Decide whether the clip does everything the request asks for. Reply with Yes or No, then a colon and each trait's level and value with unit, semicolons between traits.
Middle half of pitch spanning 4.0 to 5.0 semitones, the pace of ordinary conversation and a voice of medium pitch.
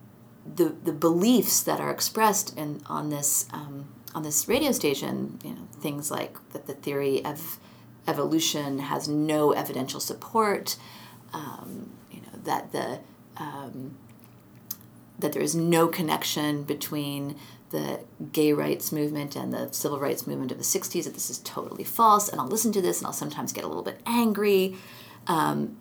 No: average, 3.5 semitones; average, 165 wpm; medium, 150 Hz